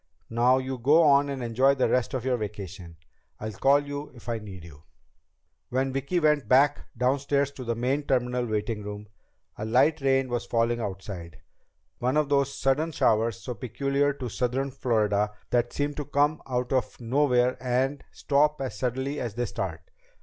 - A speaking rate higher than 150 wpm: Yes, average, 175 wpm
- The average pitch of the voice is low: Yes, low, 125 Hz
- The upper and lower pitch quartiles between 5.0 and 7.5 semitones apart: No, average, 3.4 semitones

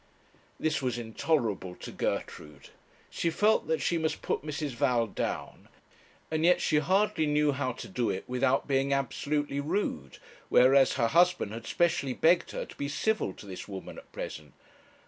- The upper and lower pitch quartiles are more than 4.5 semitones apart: Yes, average, 5.2 semitones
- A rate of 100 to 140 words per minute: No, average, 165 wpm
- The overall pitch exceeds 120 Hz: Yes, medium, 140 Hz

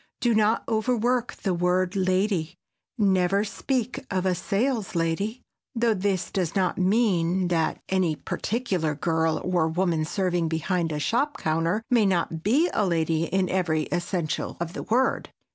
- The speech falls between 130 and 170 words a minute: Yes, average, 145 wpm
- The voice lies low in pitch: No, medium, 185 Hz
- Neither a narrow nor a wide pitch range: Yes, average, 4.3 semitones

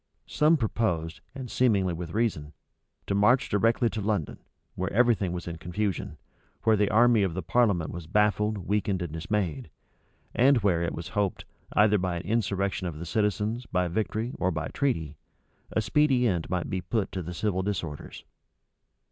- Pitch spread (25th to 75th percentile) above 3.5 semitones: Yes, average, 4.1 semitones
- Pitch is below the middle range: Yes, low, 100 Hz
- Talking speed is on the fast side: No, average, 175 wpm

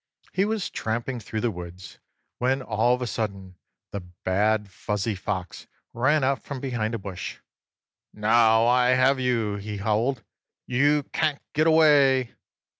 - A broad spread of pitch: No, average, 4.2 semitones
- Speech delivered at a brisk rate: No, average, 145 wpm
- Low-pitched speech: Yes, low, 115 Hz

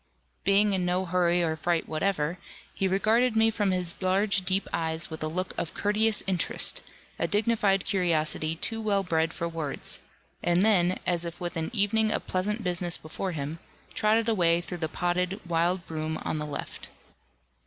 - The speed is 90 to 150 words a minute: No, average, 175 wpm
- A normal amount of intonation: Yes, average, 3.2 semitones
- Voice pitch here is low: No, medium, 180 Hz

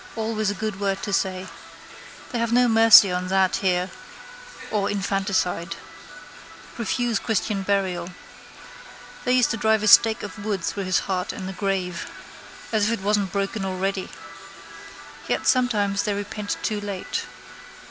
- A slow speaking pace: No, average, 145 wpm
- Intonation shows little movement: Yes, narrow, 2.3 semitones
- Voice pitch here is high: Yes, high, 200 Hz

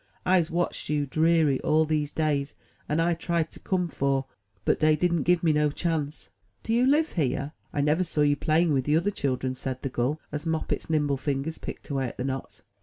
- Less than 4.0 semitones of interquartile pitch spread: Yes, average, 3.1 semitones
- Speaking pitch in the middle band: Yes, medium, 150 Hz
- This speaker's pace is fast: Yes, fast, 210 wpm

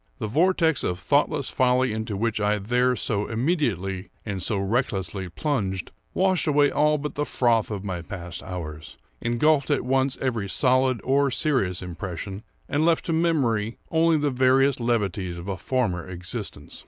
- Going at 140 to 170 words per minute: Yes, average, 160 wpm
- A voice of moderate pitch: No, low, 120 Hz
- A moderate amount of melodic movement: No, wide, 6.5 semitones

